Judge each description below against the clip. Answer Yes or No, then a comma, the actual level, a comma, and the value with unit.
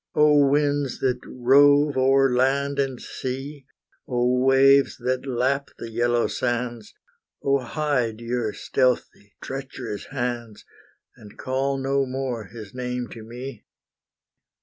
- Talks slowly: Yes, slow, 120 wpm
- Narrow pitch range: Yes, narrow, 2.2 semitones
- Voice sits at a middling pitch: No, low, 130 Hz